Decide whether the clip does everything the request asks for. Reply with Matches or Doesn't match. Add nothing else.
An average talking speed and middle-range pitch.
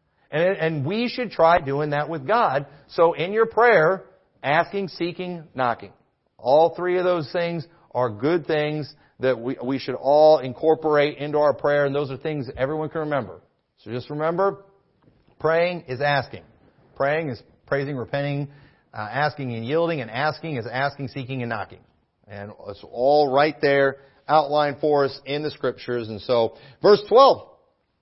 Matches